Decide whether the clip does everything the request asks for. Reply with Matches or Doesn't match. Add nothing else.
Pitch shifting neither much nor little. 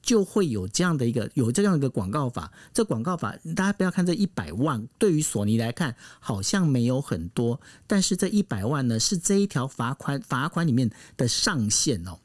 Doesn't match